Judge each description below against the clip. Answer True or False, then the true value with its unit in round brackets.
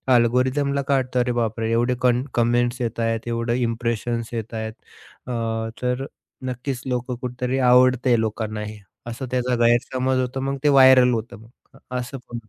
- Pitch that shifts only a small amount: True (1.6 semitones)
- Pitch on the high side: False (125 Hz)